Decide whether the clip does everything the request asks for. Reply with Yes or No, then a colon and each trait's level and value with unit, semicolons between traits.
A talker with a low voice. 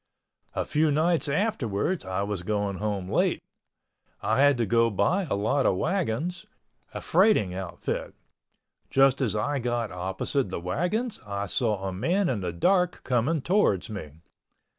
Yes: low, 115 Hz